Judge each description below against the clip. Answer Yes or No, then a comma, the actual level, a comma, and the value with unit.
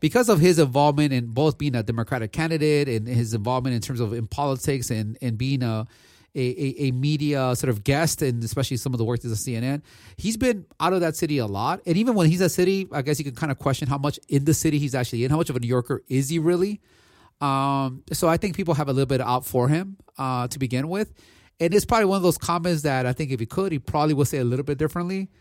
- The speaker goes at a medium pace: No, fast, 265 wpm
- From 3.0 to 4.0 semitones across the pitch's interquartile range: No, average, 4.4 semitones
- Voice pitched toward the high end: No, medium, 140 Hz